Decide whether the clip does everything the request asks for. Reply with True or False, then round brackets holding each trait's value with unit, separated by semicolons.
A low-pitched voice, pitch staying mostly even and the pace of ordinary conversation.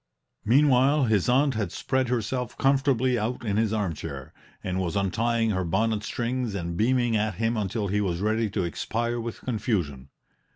False (110 Hz; 3.7 semitones; 165 wpm)